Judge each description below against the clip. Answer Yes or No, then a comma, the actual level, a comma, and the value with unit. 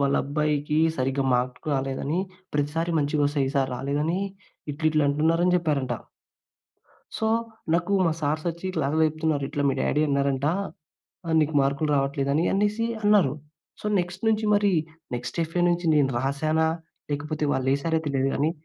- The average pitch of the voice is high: No, medium, 150 Hz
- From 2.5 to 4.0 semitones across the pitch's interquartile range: Yes, average, 3.0 semitones